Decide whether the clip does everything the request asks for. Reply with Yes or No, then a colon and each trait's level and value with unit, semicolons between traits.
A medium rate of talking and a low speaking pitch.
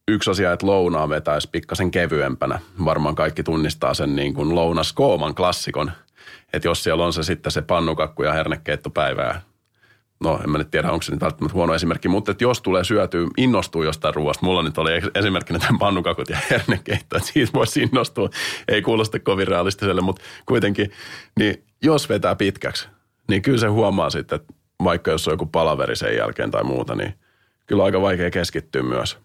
Yes: average, 180 wpm; very low, 90 Hz